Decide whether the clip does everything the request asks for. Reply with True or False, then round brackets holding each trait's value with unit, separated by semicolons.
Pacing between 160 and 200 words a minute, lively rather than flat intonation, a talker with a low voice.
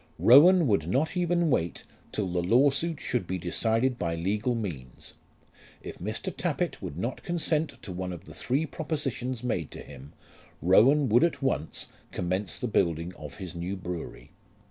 True (165 wpm; 7.8 semitones; 110 Hz)